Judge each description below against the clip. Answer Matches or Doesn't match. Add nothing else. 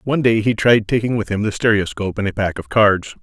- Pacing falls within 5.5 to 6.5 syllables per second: Matches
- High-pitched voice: Doesn't match